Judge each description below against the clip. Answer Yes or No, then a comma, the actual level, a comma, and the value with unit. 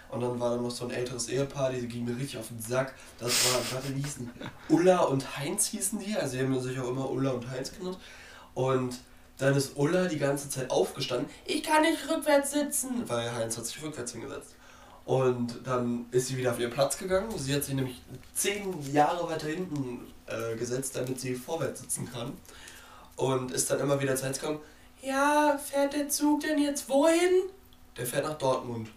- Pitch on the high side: No, low, 135 Hz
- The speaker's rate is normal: No, fast, 200 wpm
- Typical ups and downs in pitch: No, wide, 7.0 semitones